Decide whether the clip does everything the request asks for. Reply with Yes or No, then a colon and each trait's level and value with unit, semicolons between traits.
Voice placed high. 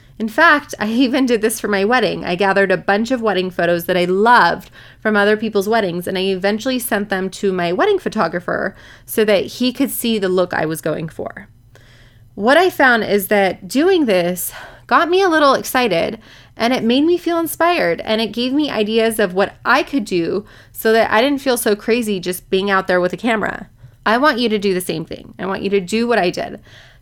Yes: high, 210 Hz